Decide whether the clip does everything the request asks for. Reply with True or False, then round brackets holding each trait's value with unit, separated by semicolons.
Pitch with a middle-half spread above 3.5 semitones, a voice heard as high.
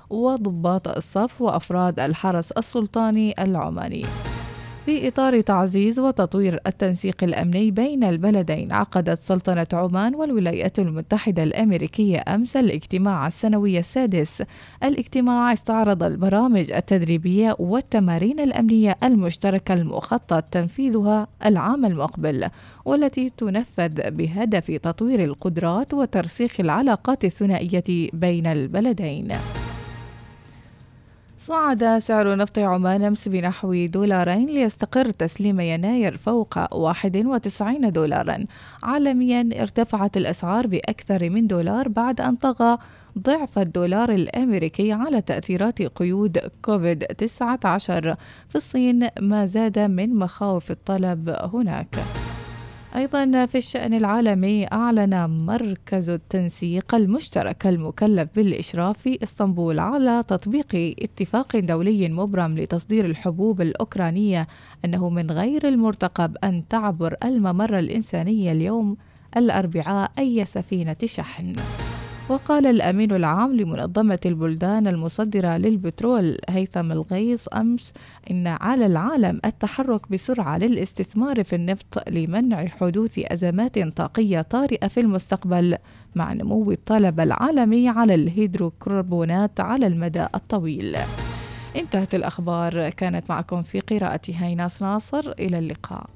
True (4.5 semitones; 195 Hz)